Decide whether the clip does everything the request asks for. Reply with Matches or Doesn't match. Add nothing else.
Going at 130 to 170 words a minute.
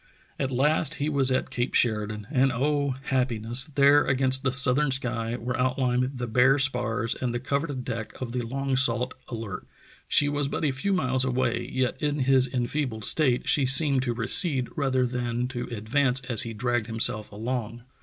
Doesn't match